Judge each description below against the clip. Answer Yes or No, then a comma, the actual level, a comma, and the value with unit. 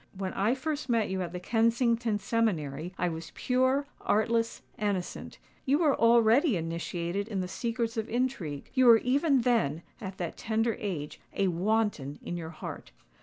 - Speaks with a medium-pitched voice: No, high, 220 Hz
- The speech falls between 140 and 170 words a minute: Yes, average, 155 wpm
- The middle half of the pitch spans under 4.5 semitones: No, average, 5.1 semitones